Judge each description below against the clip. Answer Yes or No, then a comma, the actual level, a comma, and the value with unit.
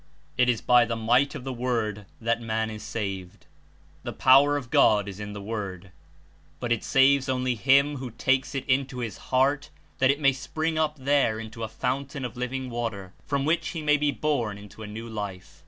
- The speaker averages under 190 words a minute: No, fast, 205 wpm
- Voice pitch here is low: Yes, low, 125 Hz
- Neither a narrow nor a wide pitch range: Yes, average, 3.9 semitones